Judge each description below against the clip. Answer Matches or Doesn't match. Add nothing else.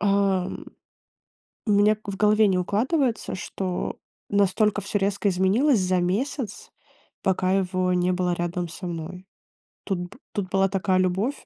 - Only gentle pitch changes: Matches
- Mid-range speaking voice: Doesn't match